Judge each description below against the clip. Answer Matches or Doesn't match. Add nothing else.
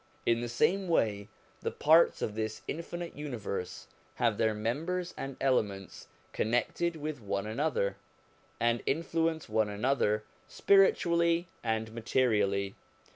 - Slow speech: Matches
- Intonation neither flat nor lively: Doesn't match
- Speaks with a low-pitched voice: Matches